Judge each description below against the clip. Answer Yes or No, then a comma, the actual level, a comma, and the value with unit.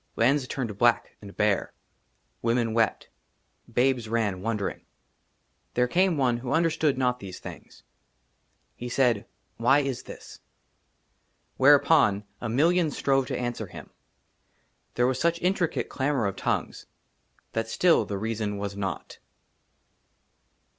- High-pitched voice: No, low, 120 Hz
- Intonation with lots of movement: No, average, 4.0 semitones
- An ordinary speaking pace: No, slow, 130 wpm